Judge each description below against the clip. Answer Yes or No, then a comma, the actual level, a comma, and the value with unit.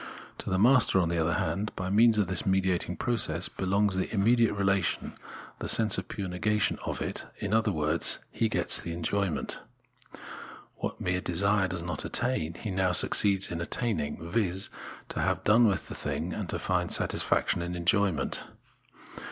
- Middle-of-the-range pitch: No, very low, 95 Hz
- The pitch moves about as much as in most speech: Yes, average, 3.3 semitones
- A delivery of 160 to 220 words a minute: Yes, average, 175 wpm